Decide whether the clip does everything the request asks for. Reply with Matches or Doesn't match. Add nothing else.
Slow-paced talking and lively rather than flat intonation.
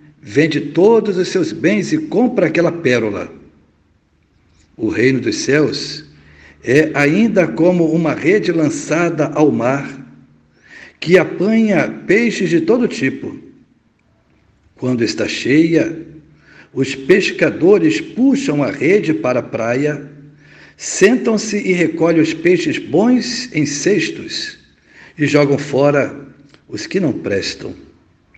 Matches